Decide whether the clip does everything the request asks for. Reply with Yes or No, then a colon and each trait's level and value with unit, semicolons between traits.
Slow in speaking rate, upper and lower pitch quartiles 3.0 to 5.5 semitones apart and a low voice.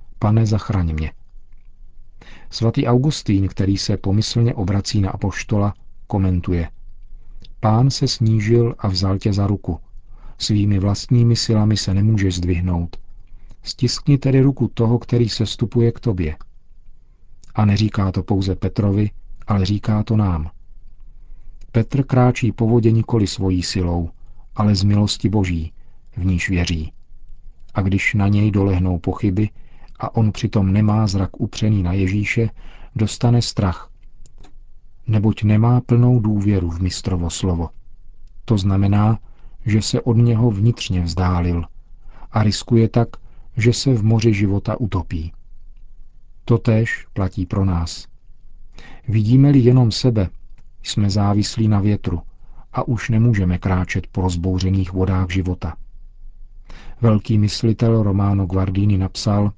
No: average, 125 wpm; average, 3.3 semitones; low, 105 Hz